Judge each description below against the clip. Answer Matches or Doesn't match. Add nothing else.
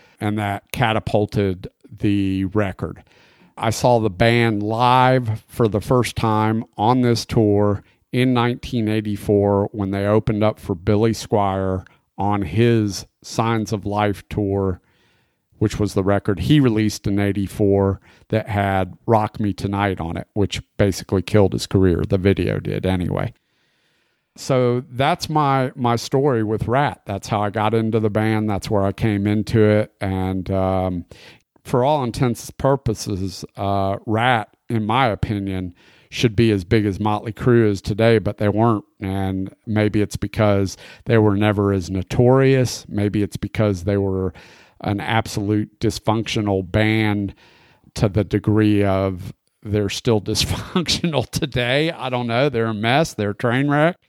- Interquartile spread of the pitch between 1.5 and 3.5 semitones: Matches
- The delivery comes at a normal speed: Matches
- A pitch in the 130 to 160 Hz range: Doesn't match